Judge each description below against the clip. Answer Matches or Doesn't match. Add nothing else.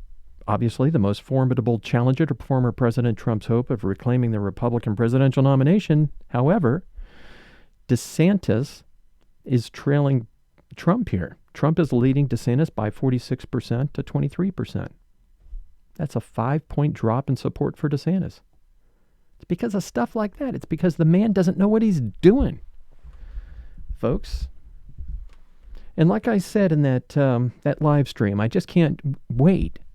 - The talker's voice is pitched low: Matches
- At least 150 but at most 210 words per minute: Doesn't match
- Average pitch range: Doesn't match